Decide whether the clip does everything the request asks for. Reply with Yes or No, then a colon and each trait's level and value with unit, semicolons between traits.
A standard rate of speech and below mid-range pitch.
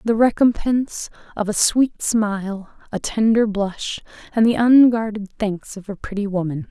No: average, 150 wpm; high, 215 Hz